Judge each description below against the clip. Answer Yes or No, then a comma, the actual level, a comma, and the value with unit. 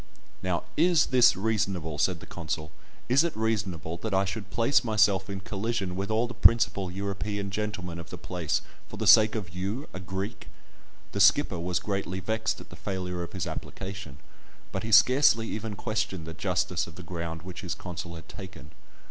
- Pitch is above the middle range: No, very low, 95 Hz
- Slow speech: No, average, 185 wpm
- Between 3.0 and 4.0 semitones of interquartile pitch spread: Yes, average, 3.6 semitones